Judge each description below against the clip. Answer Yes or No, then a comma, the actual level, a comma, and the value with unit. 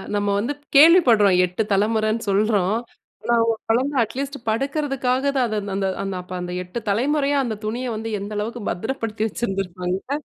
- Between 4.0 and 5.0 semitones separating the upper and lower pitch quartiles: Yes, average, 4.6 semitones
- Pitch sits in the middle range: No, high, 220 Hz